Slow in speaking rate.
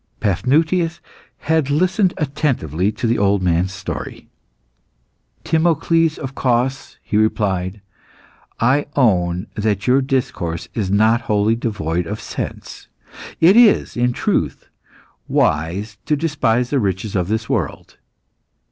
Yes: slow, 120 wpm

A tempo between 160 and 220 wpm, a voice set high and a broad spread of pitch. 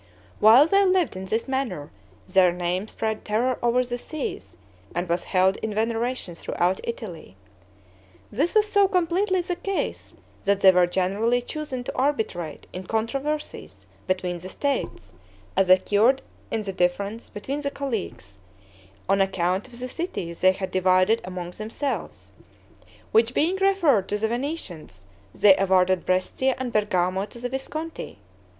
No: average, 145 wpm; high, 220 Hz; wide, 6.3 semitones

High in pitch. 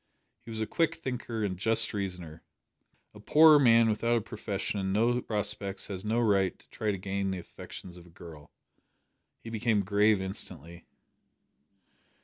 No: low, 105 Hz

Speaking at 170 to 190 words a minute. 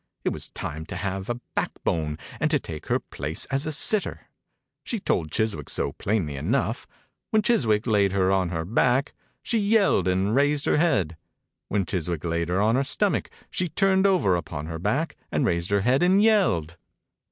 Yes: average, 185 wpm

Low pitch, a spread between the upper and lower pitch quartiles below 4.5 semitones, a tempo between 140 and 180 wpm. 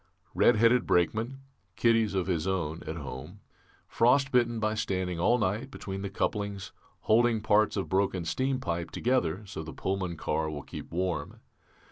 No: low, 100 Hz; average, 4.9 semitones; average, 150 wpm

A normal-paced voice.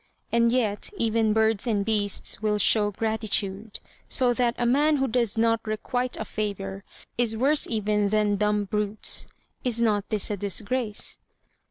Yes: average, 155 wpm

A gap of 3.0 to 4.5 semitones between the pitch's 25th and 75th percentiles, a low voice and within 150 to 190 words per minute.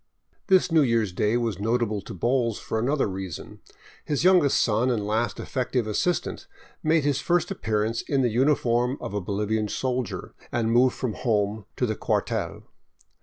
Yes: average, 3.9 semitones; low, 120 Hz; average, 170 wpm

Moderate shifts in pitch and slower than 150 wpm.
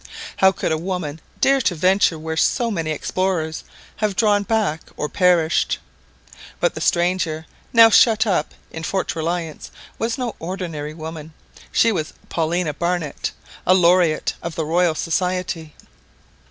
Yes: average, 3.1 semitones; average, 140 wpm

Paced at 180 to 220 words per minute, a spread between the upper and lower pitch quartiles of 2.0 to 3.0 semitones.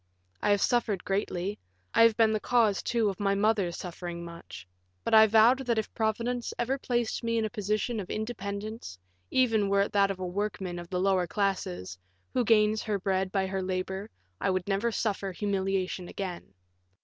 Yes: average, 185 wpm; average, 2.7 semitones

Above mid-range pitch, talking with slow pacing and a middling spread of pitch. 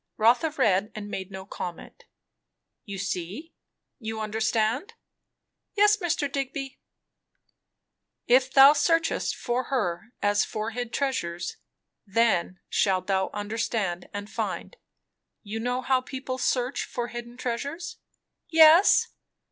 Yes: high, 235 Hz; slow, 115 wpm; average, 4.9 semitones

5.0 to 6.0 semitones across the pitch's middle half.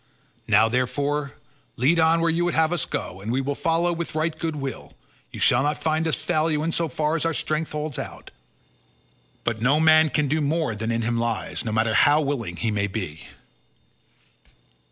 Yes: wide, 5.6 semitones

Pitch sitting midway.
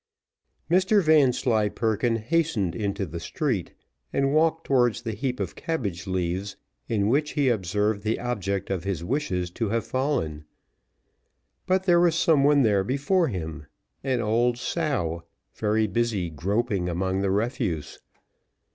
No: low, 110 Hz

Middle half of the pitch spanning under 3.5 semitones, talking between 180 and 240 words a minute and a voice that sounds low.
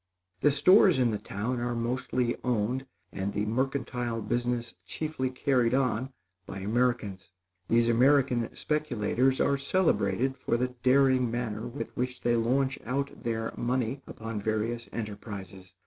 No: average, 2.7 semitones; slow, 135 wpm; low, 120 Hz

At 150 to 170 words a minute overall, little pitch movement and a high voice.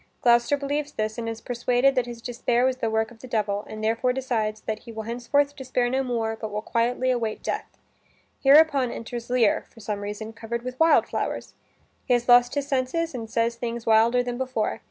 No: fast, 205 wpm; narrow, 2.3 semitones; high, 240 Hz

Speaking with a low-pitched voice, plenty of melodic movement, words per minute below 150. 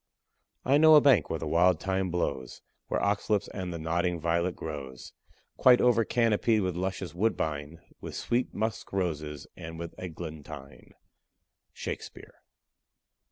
No: very low, 90 Hz; average, 4.6 semitones; average, 140 wpm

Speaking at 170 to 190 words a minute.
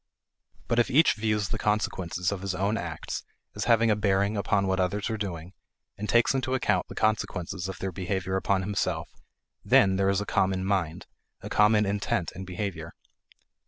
Yes: average, 180 wpm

